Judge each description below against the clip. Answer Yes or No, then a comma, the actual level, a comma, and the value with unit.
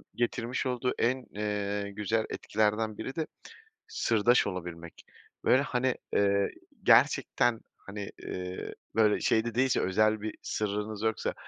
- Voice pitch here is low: Yes, low, 110 Hz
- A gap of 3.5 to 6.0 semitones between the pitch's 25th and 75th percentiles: No, average, 2.8 semitones